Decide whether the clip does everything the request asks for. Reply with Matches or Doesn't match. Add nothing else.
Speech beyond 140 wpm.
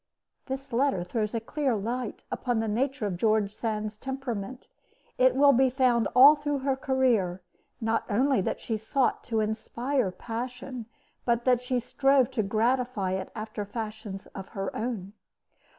Matches